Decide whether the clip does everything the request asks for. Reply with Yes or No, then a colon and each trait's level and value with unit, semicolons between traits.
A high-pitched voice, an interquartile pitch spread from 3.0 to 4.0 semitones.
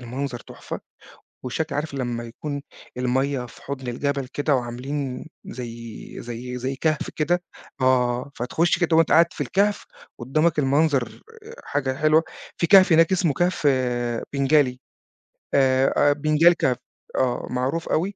No: medium, 140 Hz; average, 3.7 semitones